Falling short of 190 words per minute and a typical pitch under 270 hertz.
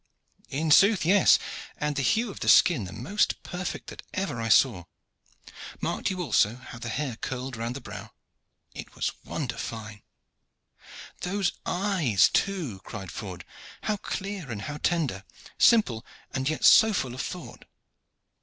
Yes: average, 155 wpm; medium, 140 Hz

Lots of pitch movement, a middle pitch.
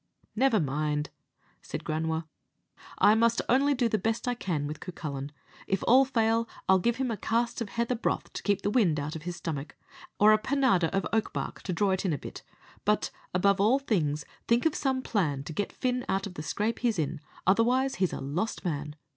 No: wide, 6.6 semitones; high, 200 Hz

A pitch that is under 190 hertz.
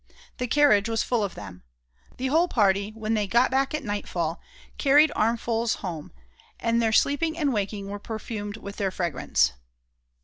No: high, 220 Hz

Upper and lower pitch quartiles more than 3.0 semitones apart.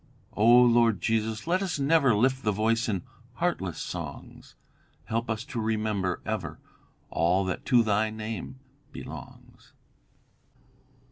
No: narrow, 2.4 semitones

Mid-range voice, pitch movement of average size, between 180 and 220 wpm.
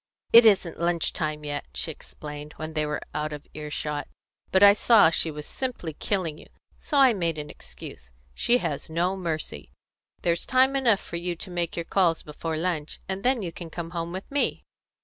Yes: medium, 170 Hz; average, 4.1 semitones; average, 200 wpm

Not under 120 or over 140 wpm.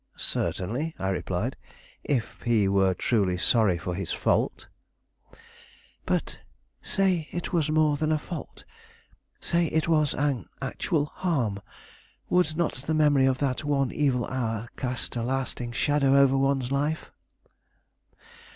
Yes: slow, 135 wpm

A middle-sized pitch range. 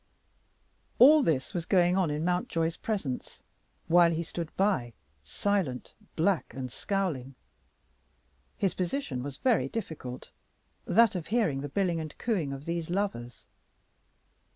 No: wide, 6.0 semitones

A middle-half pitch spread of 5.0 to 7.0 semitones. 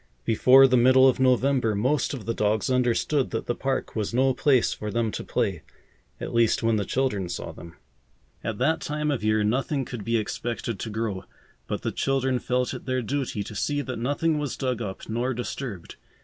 No: average, 3.3 semitones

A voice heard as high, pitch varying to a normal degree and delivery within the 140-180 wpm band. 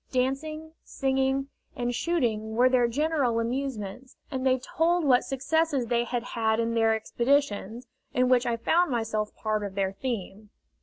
Yes: high, 245 Hz; average, 3.3 semitones; average, 155 wpm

